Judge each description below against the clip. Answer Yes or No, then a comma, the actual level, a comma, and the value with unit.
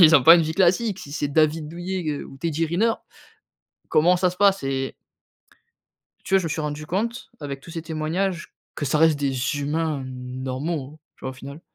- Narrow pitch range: No, average, 3.6 semitones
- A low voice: No, medium, 155 Hz